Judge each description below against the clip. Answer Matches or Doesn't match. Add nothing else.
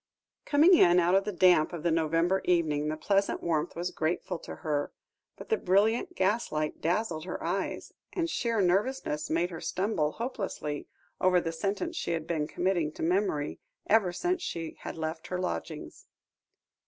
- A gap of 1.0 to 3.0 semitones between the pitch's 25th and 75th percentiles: Doesn't match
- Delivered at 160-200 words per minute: Matches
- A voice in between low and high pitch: Matches